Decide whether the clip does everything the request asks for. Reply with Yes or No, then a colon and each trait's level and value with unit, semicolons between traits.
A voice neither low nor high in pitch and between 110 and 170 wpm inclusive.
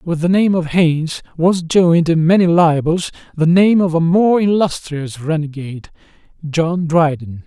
Yes: medium, 165 Hz; average, 155 wpm